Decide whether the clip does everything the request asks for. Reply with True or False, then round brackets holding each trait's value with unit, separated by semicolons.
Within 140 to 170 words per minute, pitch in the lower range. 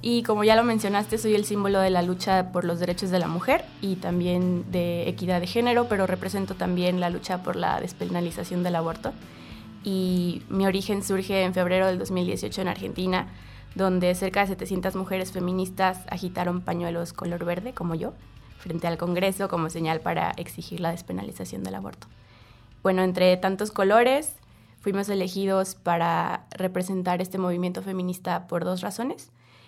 False (160 wpm; 180 Hz)